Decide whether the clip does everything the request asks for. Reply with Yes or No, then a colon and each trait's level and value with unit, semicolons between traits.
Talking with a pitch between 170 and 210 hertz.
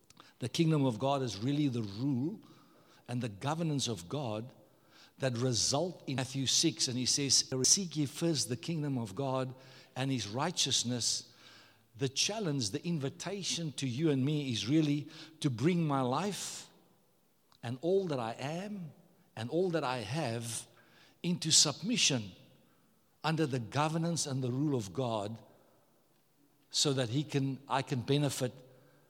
No: low, 135 Hz